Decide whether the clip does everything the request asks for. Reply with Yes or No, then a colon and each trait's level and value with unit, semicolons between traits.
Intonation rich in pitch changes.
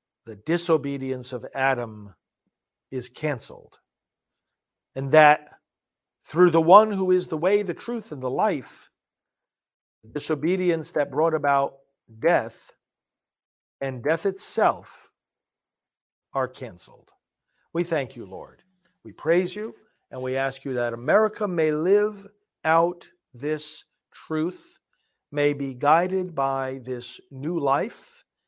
No: average, 4.8 semitones